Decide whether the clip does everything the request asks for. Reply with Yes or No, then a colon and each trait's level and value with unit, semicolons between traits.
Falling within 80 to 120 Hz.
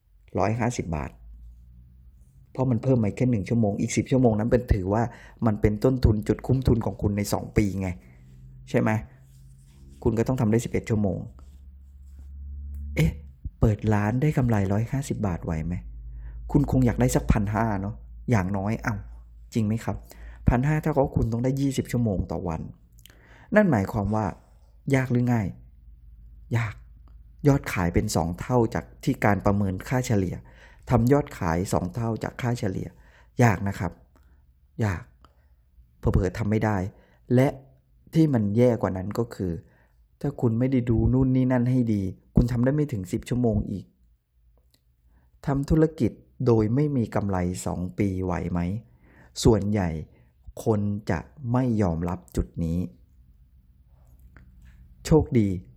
Yes: low, 100 Hz